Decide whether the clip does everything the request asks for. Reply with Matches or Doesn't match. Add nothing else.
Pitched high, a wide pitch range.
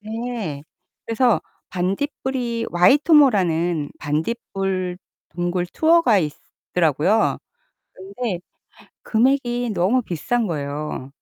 Matches